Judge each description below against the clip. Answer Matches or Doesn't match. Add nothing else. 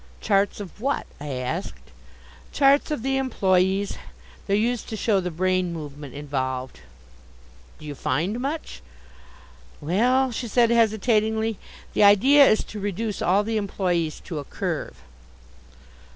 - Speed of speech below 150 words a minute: Matches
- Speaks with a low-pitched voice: Doesn't match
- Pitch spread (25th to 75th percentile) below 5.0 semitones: Doesn't match